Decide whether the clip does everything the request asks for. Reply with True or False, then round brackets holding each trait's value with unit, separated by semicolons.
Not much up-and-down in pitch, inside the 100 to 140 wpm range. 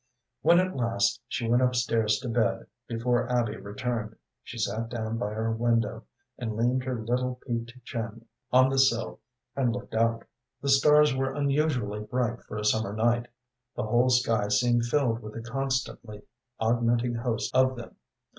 False (2.1 semitones; 165 wpm)